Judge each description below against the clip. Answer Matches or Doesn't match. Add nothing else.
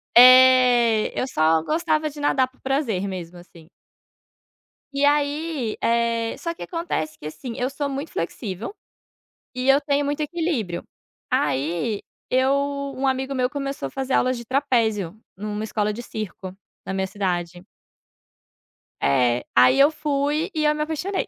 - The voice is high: Matches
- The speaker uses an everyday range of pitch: Doesn't match